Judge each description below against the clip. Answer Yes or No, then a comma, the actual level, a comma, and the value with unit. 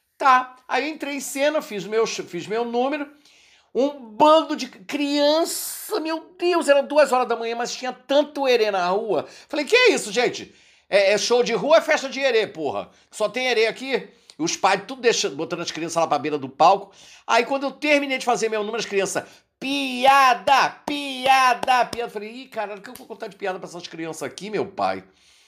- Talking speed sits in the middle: No, fast, 205 wpm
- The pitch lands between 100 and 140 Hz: No, very high, 255 Hz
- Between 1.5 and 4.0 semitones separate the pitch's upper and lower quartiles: No, average, 5.1 semitones